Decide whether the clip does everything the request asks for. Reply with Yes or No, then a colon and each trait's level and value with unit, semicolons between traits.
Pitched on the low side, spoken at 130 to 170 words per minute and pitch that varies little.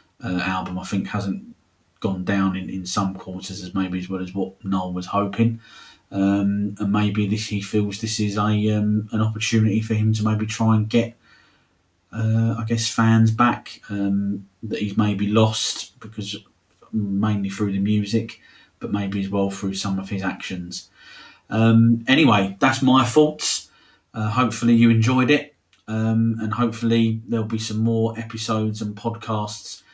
Yes: low, 105 Hz; average, 165 wpm; narrow, 2.3 semitones